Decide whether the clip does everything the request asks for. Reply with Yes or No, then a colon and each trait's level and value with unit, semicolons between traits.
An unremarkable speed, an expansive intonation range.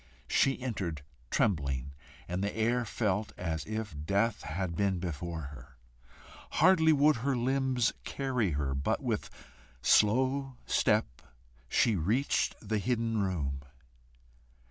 No: slow, 120 wpm; wide, 7.4 semitones